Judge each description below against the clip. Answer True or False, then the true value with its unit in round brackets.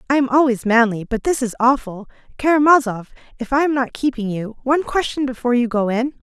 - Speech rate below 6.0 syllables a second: False (6.1 syllables/s)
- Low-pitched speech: False (250 Hz)